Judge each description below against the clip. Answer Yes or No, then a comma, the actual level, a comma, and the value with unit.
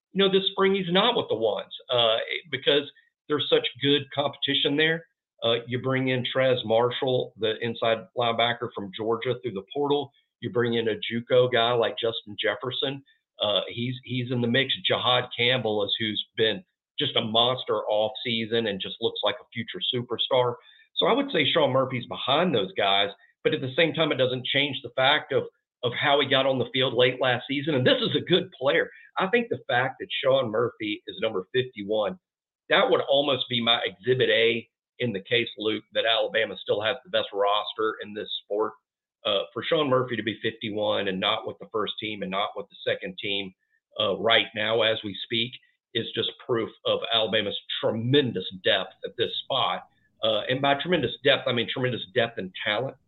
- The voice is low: Yes, low, 125 Hz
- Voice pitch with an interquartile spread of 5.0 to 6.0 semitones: Yes, wide, 5.4 semitones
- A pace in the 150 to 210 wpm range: Yes, average, 200 wpm